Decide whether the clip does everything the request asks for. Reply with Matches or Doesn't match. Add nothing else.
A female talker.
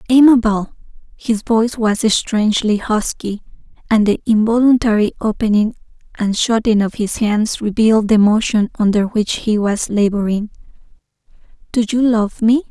Matches